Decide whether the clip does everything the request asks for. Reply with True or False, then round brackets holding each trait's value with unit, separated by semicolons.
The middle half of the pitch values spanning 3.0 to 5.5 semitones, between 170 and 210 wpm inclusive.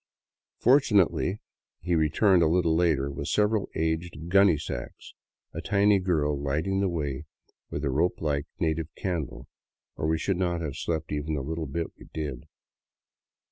False (3.6 semitones; 150 wpm)